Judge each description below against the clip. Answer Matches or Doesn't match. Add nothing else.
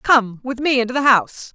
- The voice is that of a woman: Matches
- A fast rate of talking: Matches